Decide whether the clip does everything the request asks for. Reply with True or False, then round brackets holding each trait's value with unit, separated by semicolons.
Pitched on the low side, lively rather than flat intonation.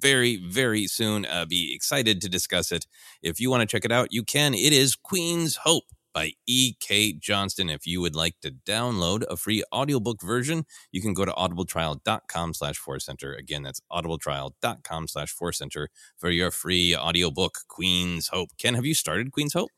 True (95 Hz; 6.6 semitones)